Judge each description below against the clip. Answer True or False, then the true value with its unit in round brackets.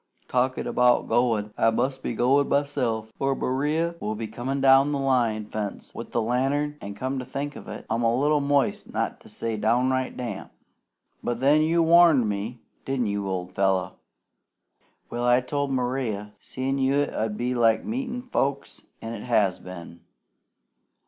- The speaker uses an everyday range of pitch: True (3.8 semitones)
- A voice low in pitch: True (125 Hz)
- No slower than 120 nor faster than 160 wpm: False (170 wpm)